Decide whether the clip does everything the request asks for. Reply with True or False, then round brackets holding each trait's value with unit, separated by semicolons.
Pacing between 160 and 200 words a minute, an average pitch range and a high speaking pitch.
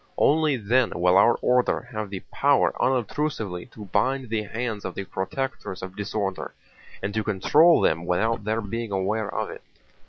False (165 wpm; 4.5 semitones; 110 Hz)